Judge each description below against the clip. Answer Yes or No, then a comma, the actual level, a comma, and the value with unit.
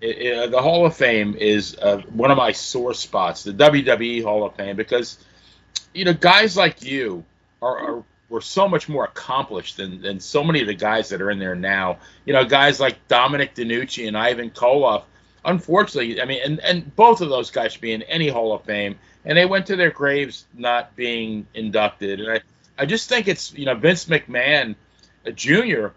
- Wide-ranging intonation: Yes, wide, 6.1 semitones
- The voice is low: Yes, low, 120 Hz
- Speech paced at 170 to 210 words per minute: Yes, fast, 205 wpm